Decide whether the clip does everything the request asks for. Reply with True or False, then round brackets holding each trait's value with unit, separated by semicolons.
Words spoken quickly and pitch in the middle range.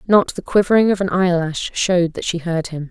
True (225 wpm; 180 Hz)